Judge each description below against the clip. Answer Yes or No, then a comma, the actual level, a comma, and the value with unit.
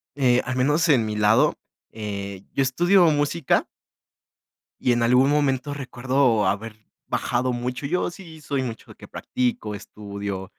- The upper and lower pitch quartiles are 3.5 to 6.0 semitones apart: Yes, average, 4.8 semitones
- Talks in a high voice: No, low, 125 Hz